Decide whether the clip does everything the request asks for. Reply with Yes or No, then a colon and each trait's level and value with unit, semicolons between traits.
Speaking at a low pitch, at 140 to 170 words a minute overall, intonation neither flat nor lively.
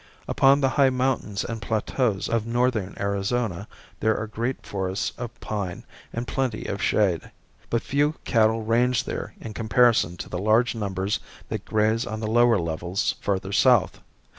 Yes: low, 110 Hz; average, 160 wpm; average, 3.3 semitones